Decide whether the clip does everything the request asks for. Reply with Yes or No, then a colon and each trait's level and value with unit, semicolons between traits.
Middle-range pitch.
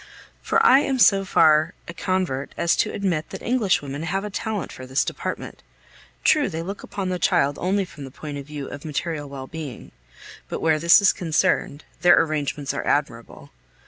Yes: medium, 165 Hz